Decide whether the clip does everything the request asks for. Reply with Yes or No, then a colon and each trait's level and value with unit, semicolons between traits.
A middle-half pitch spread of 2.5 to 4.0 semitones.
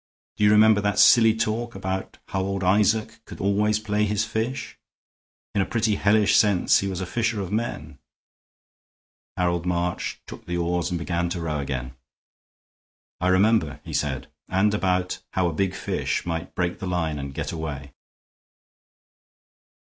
Yes: average, 3.4 semitones